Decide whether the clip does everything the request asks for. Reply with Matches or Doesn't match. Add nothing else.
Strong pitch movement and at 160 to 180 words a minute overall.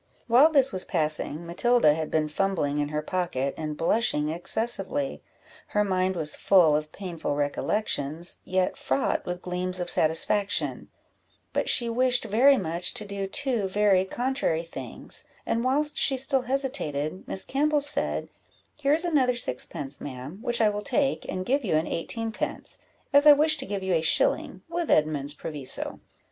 Matches